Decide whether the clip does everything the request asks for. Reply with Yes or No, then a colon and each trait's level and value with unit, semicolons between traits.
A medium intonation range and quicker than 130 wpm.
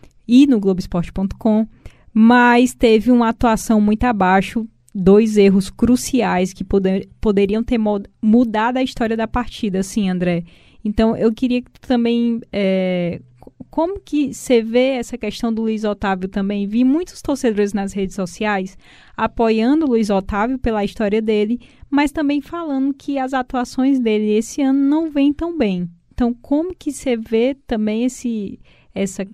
Yes: average, 3.7 semitones; average, 155 wpm